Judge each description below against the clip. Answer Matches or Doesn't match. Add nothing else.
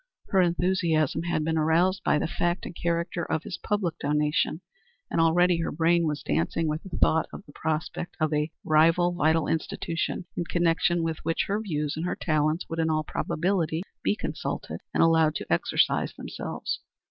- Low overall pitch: Doesn't match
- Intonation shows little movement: Matches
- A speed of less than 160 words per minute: Doesn't match